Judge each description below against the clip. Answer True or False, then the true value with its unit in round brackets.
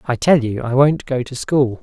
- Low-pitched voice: True (130 Hz)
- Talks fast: True (265 wpm)